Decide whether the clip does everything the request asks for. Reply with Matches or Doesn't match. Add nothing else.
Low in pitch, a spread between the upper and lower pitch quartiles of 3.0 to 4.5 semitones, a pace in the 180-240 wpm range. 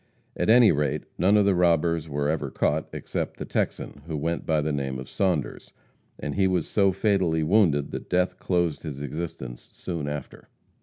Matches